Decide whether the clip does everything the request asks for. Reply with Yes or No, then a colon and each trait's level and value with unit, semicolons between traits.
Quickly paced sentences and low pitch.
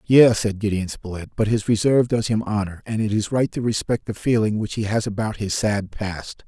Yes: fast, 230 wpm; low, 105 Hz